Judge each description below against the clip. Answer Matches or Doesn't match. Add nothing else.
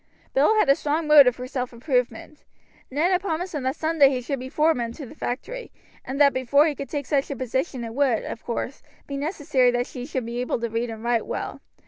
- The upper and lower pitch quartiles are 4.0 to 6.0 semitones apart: Doesn't match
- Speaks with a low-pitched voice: Doesn't match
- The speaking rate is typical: Doesn't match